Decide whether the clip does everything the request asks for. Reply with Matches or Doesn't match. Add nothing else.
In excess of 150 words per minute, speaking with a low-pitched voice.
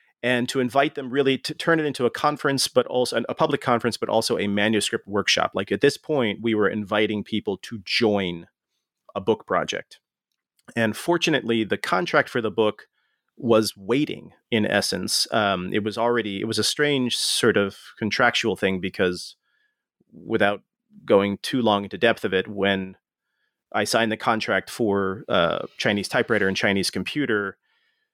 Matches